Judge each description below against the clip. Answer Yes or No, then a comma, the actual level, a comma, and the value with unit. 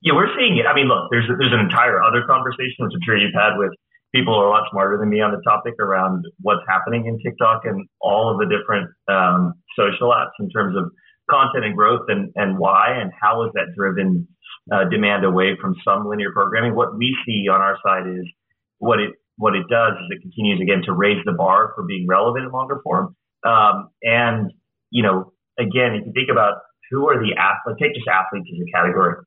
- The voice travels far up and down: No, average, 4.2 semitones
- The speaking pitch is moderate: No, low, 105 Hz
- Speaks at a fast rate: Yes, fast, 225 wpm